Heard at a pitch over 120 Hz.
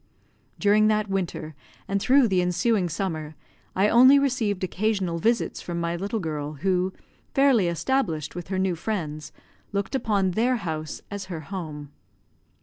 Yes: high, 190 Hz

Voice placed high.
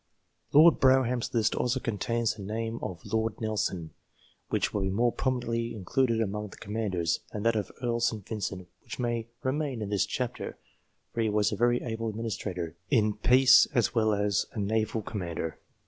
No: low, 110 Hz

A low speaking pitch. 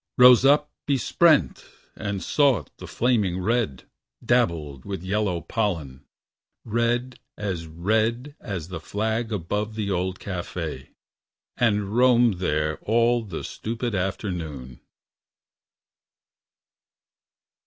Yes: low, 105 Hz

